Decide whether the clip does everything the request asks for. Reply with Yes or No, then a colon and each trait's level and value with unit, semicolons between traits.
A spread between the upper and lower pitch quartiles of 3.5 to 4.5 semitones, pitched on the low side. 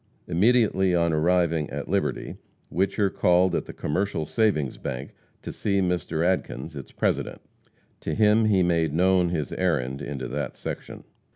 Yes: average, 3.9 semitones; very low, 85 Hz